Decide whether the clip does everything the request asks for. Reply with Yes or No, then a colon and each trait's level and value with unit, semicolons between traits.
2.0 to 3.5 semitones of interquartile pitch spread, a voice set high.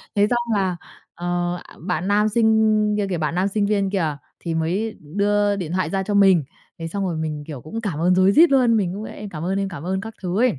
Yes: average, 3.2 semitones; high, 195 Hz